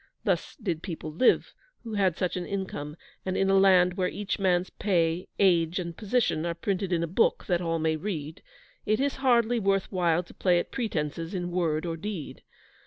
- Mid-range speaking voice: Yes, medium, 180 Hz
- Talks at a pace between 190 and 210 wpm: Yes, average, 195 wpm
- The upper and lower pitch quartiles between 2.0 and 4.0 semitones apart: Yes, average, 3.1 semitones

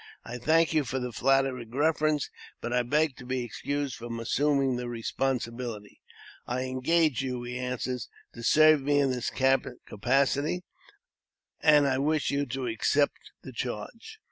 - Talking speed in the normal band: Yes, average, 150 wpm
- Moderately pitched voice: No, low, 130 Hz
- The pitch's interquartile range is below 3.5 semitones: Yes, average, 2.8 semitones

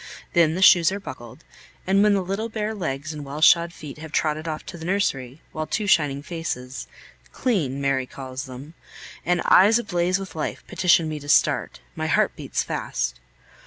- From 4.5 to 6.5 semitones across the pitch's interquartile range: Yes, average, 5.2 semitones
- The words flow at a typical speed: Yes, average, 185 wpm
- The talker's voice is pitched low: No, medium, 160 Hz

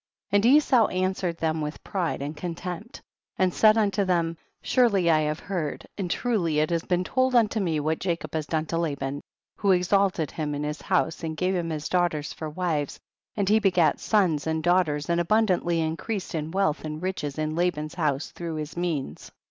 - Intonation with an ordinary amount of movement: Yes, average, 3.4 semitones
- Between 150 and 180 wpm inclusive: No, average, 195 wpm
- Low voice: No, medium, 170 Hz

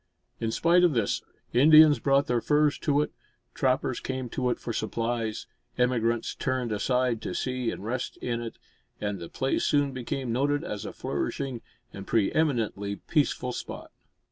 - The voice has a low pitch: Yes, low, 125 Hz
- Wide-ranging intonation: No, average, 3.4 semitones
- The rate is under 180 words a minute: Yes, average, 165 wpm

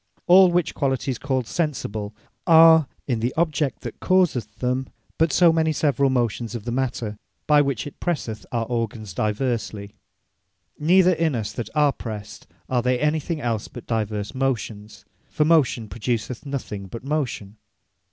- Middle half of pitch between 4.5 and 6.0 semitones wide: Yes, average, 5.3 semitones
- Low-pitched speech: Yes, low, 130 Hz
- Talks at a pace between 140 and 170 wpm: Yes, average, 150 wpm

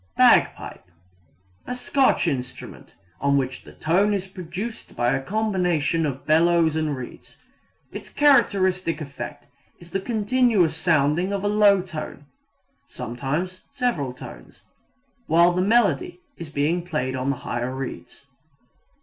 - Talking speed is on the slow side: Yes, slow, 130 wpm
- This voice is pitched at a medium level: Yes, medium, 170 Hz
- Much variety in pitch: Yes, wide, 6.0 semitones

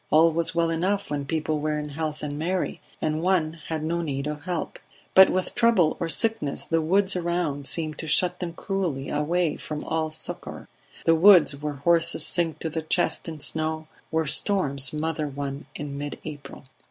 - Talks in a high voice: No, medium, 160 Hz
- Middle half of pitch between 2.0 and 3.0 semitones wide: Yes, narrow, 2.4 semitones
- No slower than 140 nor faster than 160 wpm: No, average, 185 wpm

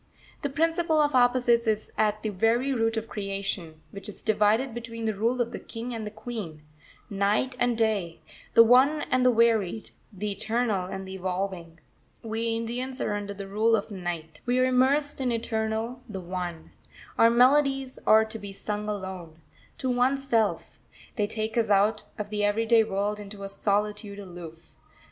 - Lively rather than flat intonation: No, average, 3.3 semitones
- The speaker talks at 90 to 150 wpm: No, average, 175 wpm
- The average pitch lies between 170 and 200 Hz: No, high, 220 Hz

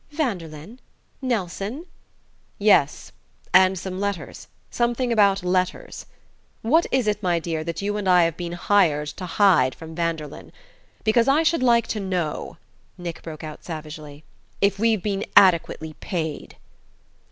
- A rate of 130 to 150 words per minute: Yes, average, 140 wpm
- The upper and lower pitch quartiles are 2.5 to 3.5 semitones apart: No, average, 4.5 semitones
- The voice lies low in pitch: No, medium, 185 Hz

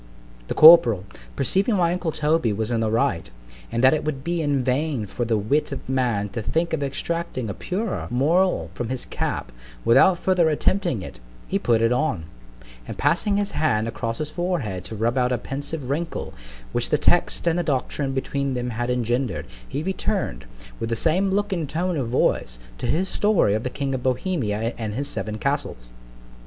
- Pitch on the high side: No, low, 135 Hz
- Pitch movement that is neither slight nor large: No, wide, 6.5 semitones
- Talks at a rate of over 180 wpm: Yes, average, 195 wpm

